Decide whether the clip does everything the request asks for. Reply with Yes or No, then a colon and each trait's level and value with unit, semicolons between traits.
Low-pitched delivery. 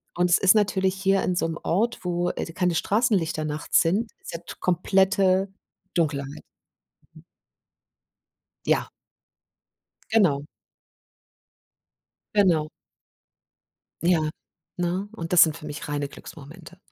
No: medium, 175 Hz